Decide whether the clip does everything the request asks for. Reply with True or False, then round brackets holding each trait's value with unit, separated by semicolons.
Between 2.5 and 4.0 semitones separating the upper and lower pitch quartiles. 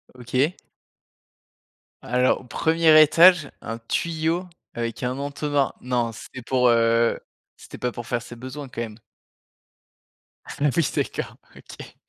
False (4.5 semitones)